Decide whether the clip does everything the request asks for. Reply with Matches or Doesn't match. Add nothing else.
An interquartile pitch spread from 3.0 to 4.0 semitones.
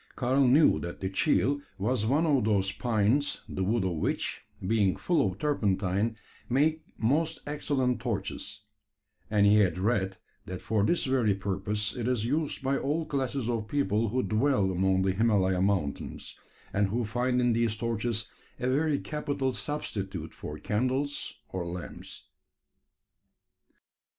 Doesn't match